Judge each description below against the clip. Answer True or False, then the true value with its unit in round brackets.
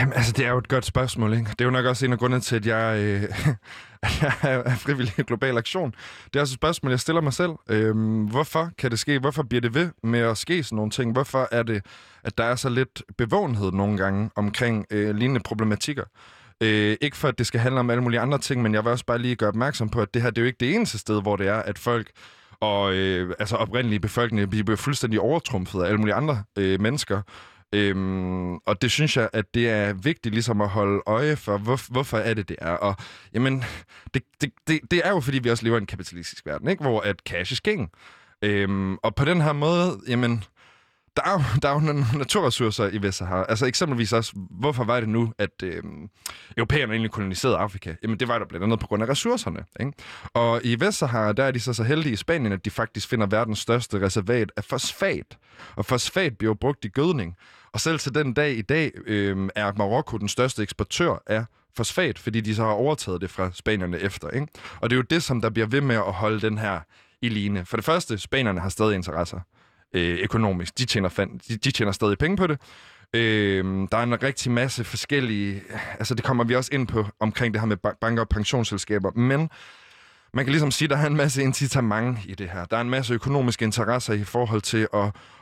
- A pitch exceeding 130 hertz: False (115 Hz)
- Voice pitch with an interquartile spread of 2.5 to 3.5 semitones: False (4.0 semitones)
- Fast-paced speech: True (235 wpm)